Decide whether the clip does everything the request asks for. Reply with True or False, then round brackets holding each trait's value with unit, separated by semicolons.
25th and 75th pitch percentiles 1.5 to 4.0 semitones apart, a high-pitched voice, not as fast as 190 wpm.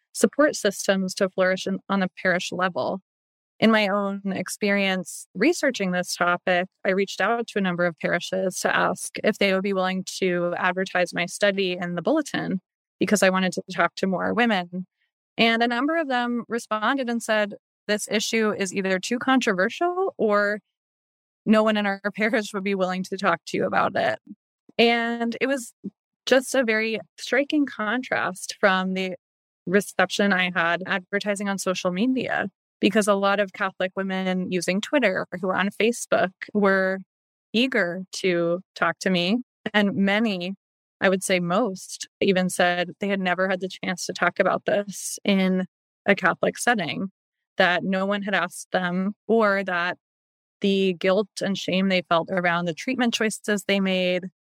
True (2.8 semitones; 195 Hz; 170 wpm)